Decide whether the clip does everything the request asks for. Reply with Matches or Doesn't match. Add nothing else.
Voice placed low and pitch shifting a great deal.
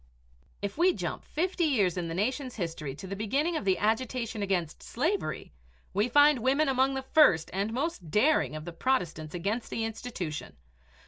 Doesn't match